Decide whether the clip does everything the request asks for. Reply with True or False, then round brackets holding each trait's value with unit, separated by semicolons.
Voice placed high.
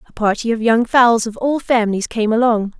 True (230 Hz)